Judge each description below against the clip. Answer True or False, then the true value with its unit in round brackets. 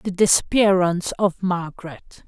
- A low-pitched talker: False (185 Hz)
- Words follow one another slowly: True (105 wpm)